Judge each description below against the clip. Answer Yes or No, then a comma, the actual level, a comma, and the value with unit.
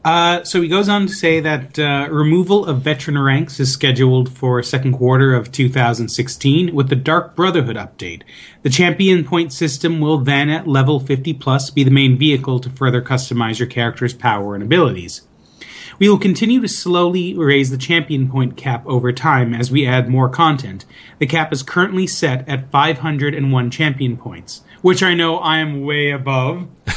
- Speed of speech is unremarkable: Yes, average, 180 wpm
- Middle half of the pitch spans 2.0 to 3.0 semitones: No, average, 4.0 semitones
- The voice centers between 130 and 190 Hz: Yes, medium, 140 Hz